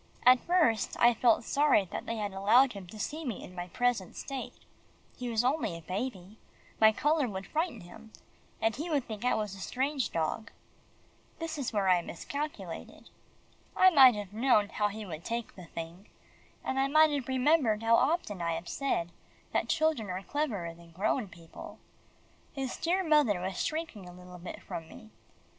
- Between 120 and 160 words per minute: No, average, 185 wpm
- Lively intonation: Yes, wide, 6.5 semitones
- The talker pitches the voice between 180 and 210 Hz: No, high, 225 Hz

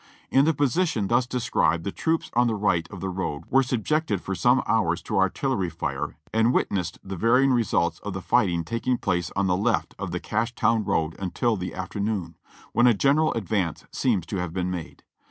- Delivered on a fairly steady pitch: No, wide, 5.4 semitones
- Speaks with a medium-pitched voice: No, low, 105 Hz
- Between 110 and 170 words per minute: No, average, 200 wpm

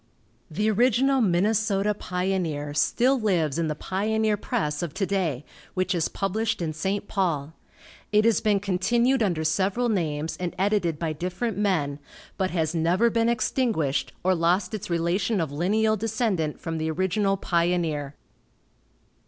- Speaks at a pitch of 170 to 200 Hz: Yes, medium, 185 Hz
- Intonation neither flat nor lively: Yes, average, 4.7 semitones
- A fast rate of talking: No, average, 145 wpm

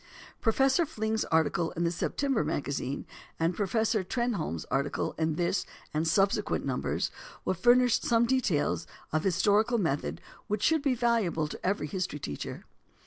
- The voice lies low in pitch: No, high, 195 Hz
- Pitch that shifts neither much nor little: No, wide, 6.5 semitones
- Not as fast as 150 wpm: Yes, average, 140 wpm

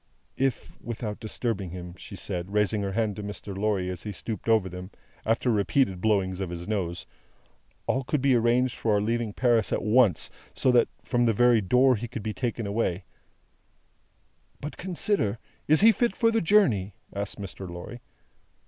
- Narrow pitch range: No, average, 4.0 semitones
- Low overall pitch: Yes, low, 110 Hz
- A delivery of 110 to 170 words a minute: No, average, 180 wpm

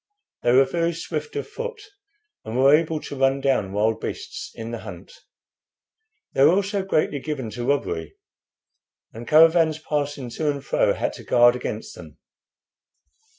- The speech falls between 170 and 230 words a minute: No, average, 155 wpm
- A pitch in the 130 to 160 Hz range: Yes, medium, 140 Hz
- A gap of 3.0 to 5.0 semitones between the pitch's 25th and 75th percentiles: Yes, average, 4.6 semitones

